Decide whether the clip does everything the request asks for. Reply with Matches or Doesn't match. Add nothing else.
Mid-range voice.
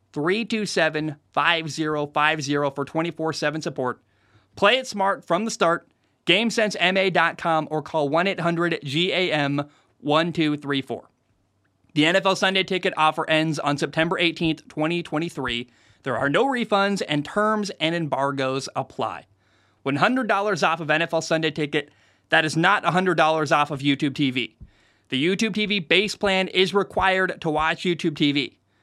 Matches